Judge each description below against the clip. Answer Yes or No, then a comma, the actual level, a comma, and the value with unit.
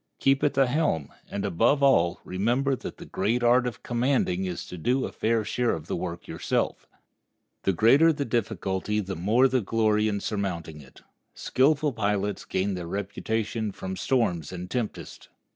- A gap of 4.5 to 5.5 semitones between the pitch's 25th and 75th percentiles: Yes, average, 4.8 semitones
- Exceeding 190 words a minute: No, average, 170 wpm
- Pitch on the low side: Yes, low, 110 Hz